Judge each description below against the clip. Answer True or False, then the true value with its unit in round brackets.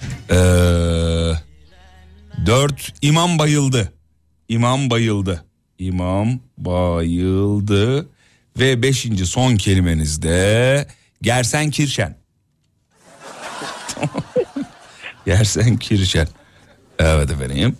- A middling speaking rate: False (65 wpm)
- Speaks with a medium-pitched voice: False (105 Hz)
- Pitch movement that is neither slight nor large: False (6.9 semitones)